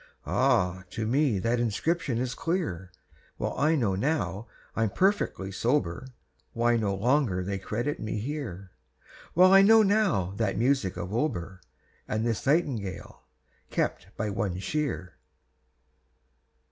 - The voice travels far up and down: Yes, wide, 7.5 semitones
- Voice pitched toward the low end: Yes, low, 115 Hz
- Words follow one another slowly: Yes, slow, 130 wpm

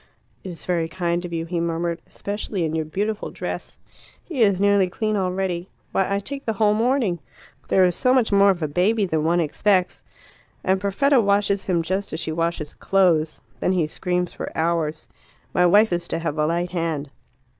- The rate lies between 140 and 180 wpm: No, average, 195 wpm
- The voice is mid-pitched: Yes, medium, 180 Hz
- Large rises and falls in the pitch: No, average, 3.2 semitones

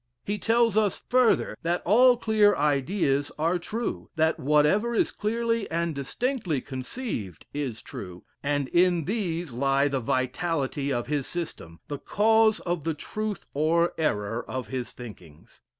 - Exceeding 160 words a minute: No, average, 145 wpm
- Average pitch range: No, wide, 7.4 semitones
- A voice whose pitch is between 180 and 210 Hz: No, medium, 160 Hz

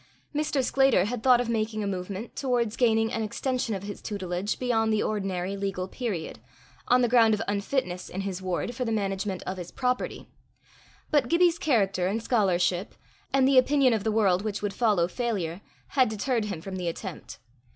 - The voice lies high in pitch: Yes, high, 215 Hz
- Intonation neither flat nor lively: Yes, average, 4.4 semitones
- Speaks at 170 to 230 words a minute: Yes, average, 185 wpm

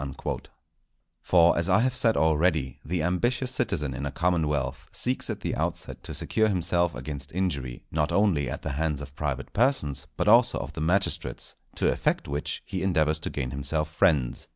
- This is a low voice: Yes, very low, 80 Hz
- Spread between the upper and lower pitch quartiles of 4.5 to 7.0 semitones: Yes, average, 4.8 semitones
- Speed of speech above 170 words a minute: Yes, average, 180 wpm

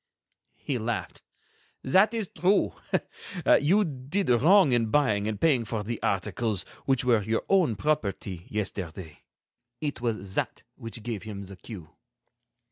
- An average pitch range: No, wide, 6.1 semitones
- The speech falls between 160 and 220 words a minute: No, slow, 135 wpm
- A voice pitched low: Yes, low, 115 Hz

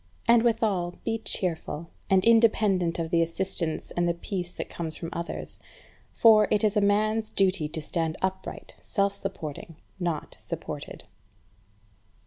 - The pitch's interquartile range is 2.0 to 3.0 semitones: No, average, 4.1 semitones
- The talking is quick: No, average, 140 wpm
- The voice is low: No, high, 190 Hz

